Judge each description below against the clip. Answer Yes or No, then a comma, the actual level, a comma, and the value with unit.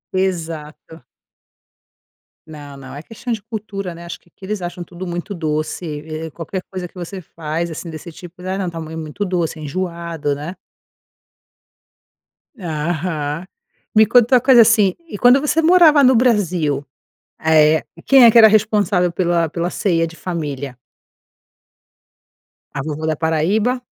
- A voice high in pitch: No, medium, 175 Hz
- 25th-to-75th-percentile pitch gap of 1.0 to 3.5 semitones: No, average, 4.5 semitones